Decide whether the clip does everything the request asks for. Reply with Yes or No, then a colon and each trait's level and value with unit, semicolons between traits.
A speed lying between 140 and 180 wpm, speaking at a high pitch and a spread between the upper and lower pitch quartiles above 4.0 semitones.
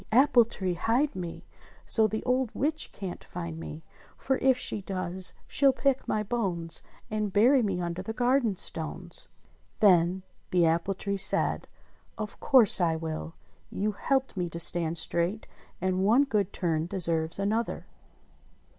Yes: average, 150 wpm; high, 195 Hz; average, 5.3 semitones